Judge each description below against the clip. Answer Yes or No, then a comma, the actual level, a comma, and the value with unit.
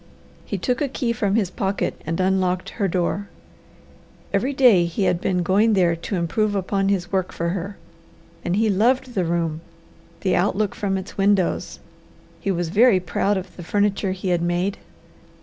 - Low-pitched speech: No, high, 190 Hz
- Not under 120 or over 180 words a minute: Yes, average, 175 wpm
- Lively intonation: No, narrow, 2.6 semitones